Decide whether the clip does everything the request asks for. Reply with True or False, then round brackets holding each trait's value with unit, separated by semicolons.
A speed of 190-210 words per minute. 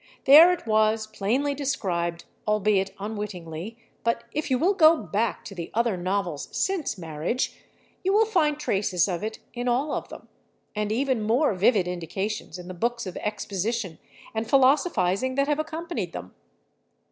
False (160 wpm)